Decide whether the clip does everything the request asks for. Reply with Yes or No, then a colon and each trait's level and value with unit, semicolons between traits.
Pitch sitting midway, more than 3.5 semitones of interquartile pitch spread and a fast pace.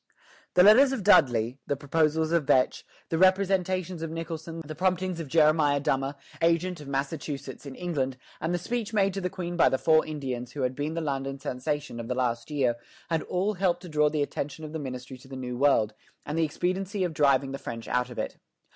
Yes: medium, 155 Hz; average, 4.6 semitones; fast, 215 wpm